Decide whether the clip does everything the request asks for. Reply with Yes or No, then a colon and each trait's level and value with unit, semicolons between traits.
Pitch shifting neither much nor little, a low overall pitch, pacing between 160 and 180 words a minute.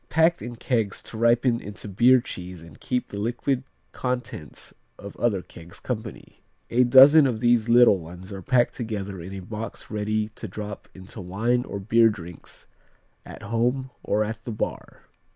Yes: average, 3.6 semitones; low, 110 Hz; average, 170 wpm